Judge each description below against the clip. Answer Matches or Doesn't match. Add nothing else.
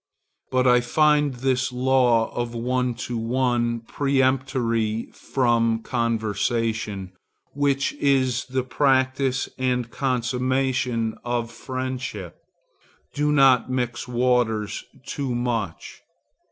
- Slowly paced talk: Matches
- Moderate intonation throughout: Doesn't match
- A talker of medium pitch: Doesn't match